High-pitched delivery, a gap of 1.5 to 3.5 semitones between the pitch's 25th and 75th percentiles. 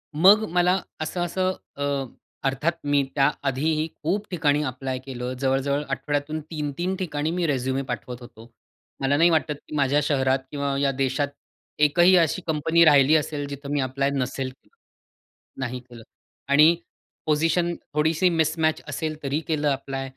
No: medium, 145 Hz; average, 3.0 semitones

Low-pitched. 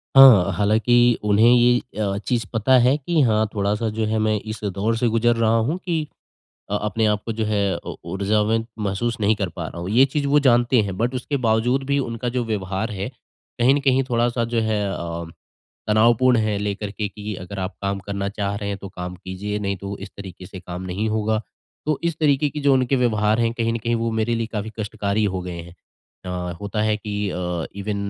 Yes: low, 110 Hz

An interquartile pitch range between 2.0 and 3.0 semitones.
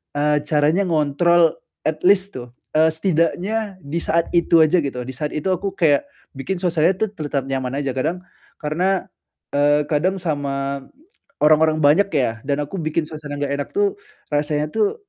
No: average, 3.8 semitones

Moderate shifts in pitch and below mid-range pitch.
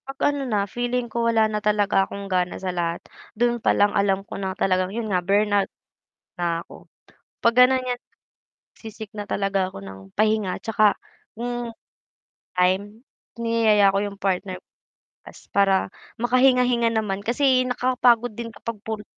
No: average, 3.4 semitones; high, 210 Hz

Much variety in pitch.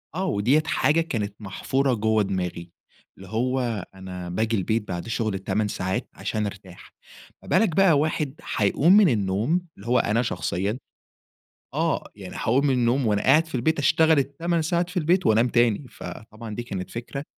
Yes: wide, 6.4 semitones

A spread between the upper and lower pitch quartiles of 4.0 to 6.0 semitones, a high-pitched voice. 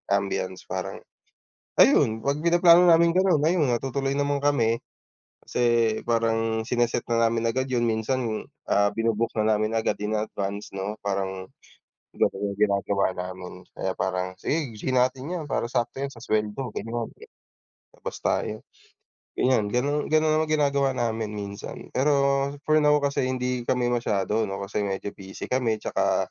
No: average, 4.6 semitones; low, 115 Hz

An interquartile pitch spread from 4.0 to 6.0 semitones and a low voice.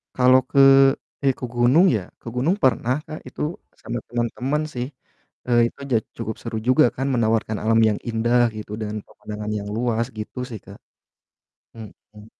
No: narrow, 2.6 semitones; low, 120 Hz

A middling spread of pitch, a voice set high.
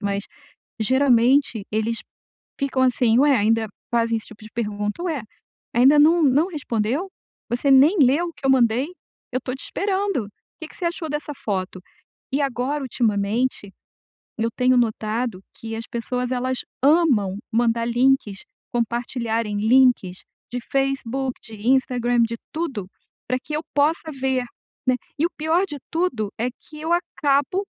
Yes: average, 4.0 semitones; very high, 250 Hz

